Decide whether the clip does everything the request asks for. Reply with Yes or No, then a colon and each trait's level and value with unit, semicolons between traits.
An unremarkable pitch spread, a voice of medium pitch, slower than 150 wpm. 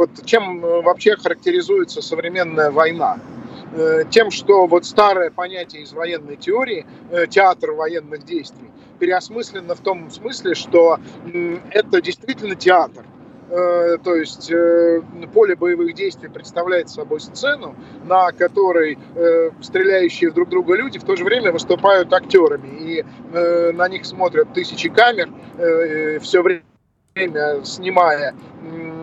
No: wide, 6.3 semitones; medium, 180 Hz; slow, 110 wpm